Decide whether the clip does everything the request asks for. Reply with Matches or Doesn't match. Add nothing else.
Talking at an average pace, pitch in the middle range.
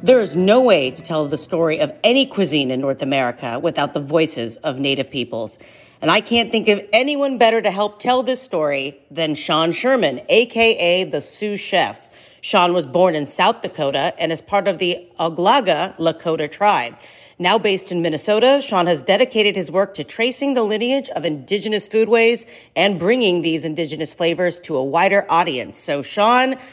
Matches